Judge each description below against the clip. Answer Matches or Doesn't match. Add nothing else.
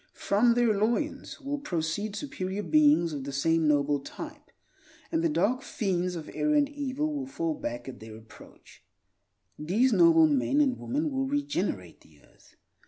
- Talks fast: Doesn't match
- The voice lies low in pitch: Doesn't match